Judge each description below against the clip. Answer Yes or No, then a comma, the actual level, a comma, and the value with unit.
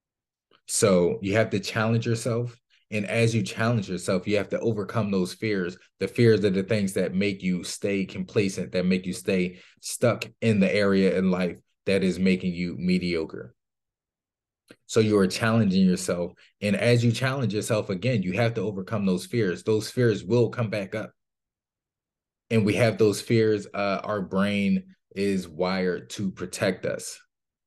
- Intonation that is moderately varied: Yes, average, 3.3 semitones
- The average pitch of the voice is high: No, low, 100 Hz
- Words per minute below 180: Yes, average, 170 wpm